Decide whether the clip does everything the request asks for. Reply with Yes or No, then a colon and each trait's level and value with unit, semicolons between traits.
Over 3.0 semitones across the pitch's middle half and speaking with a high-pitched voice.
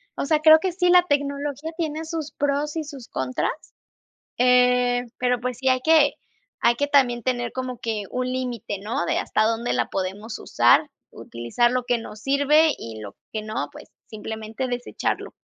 Yes: average, 4.1 semitones; very high, 250 Hz